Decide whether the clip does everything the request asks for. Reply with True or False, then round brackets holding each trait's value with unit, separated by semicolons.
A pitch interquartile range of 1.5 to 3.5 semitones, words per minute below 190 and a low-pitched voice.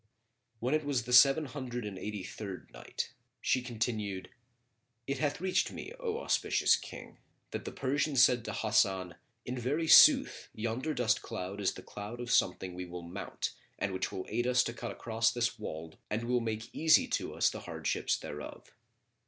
False (4.2 semitones; 180 wpm; 115 Hz)